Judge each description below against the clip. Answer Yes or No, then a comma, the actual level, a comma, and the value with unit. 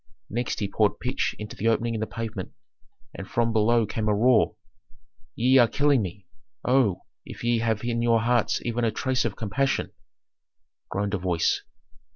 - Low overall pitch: Yes, low, 115 Hz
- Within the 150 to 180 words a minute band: Yes, average, 175 wpm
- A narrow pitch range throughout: Yes, narrow, 2.3 semitones